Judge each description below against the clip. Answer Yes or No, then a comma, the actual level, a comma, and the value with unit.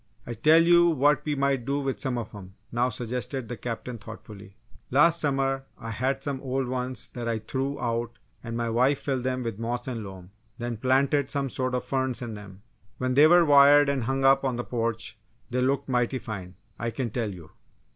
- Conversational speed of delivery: No, fast, 210 wpm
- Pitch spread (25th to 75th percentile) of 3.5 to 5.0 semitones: No, average, 2.8 semitones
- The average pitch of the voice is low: Yes, low, 125 Hz